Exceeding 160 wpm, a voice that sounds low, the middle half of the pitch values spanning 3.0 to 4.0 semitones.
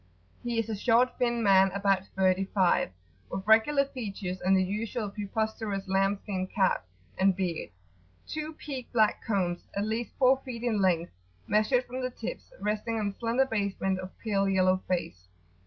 No: average, 170 wpm; high, 205 Hz; average, 3.5 semitones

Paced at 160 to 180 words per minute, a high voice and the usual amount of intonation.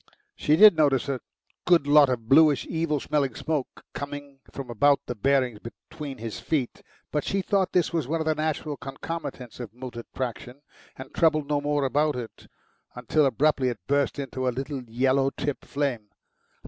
No: average, 175 wpm; medium, 140 Hz; average, 3.0 semitones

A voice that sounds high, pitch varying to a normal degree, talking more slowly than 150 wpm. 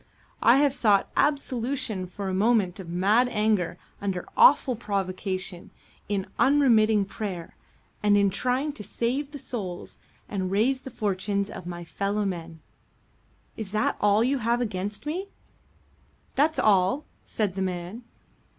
Yes: high, 210 Hz; average, 4.7 semitones; average, 140 wpm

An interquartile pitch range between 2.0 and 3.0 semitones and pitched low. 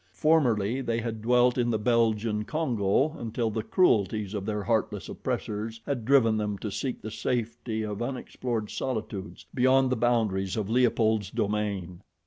Yes: narrow, 2.6 semitones; low, 110 Hz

